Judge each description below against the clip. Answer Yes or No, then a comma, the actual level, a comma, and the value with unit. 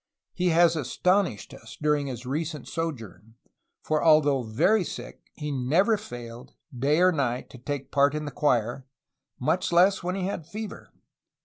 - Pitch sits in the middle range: Yes, medium, 150 Hz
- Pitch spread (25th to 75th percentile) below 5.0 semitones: No, wide, 5.4 semitones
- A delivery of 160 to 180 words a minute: Yes, average, 165 wpm